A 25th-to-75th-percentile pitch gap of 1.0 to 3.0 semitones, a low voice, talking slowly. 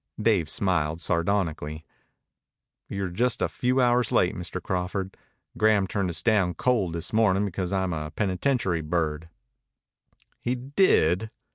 No: average, 4.4 semitones; very low, 95 Hz; slow, 130 wpm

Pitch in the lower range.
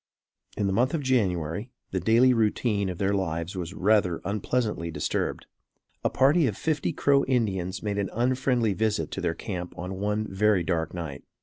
Yes: low, 100 Hz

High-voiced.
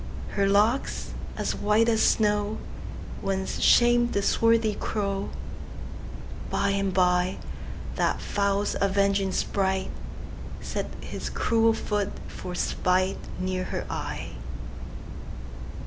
Yes: high, 200 Hz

